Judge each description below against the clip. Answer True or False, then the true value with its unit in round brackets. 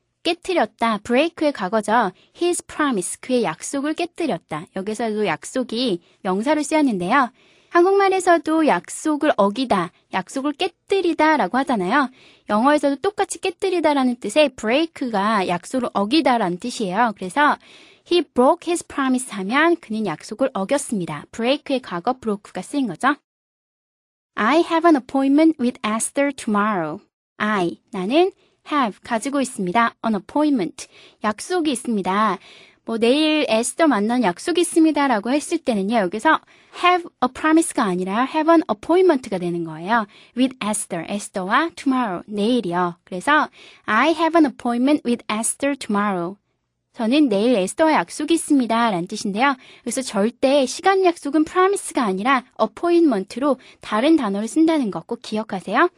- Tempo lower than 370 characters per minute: False (450 characters per minute)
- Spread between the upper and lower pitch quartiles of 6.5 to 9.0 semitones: True (6.8 semitones)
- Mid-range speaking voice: False (260 Hz)